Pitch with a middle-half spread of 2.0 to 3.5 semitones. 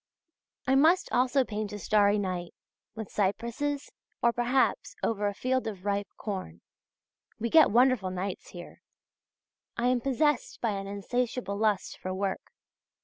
No: average, 4.0 semitones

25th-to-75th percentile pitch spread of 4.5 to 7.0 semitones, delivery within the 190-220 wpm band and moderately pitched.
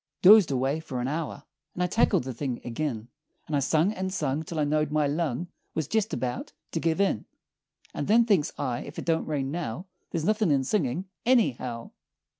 Yes: average, 5.0 semitones; average, 200 wpm; medium, 155 Hz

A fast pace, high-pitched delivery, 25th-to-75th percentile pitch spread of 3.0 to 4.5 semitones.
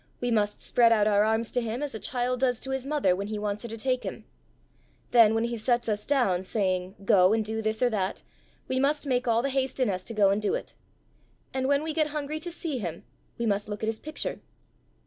Yes: fast, 245 wpm; high, 230 Hz; average, 3.9 semitones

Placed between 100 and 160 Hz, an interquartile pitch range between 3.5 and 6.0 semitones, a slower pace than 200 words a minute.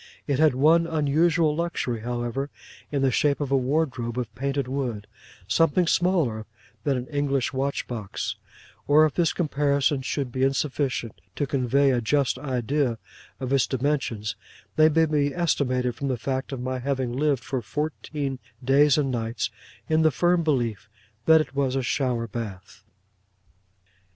No: low, 135 Hz; average, 3.1 semitones; average, 155 wpm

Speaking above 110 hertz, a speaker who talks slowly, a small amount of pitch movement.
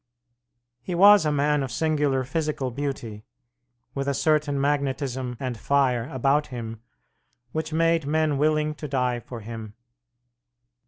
No: medium, 140 Hz; slow, 130 wpm; average, 3.3 semitones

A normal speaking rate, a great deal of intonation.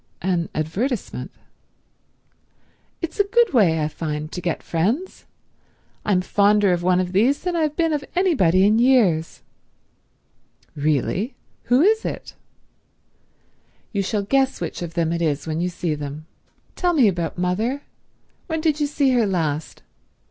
Yes: average, 150 wpm; wide, 8.7 semitones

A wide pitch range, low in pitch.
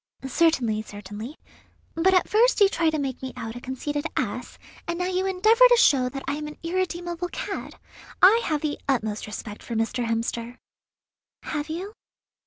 No: wide, 7.0 semitones; very high, 300 Hz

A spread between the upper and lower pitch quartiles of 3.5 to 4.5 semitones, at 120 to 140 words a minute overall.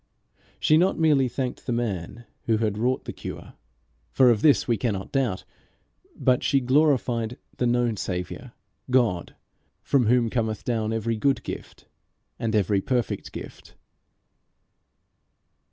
No: average, 3.0 semitones; slow, 135 wpm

